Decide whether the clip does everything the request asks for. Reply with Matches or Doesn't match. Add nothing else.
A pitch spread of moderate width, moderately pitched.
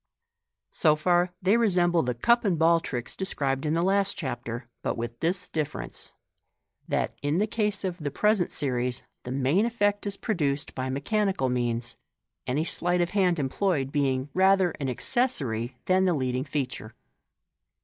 Doesn't match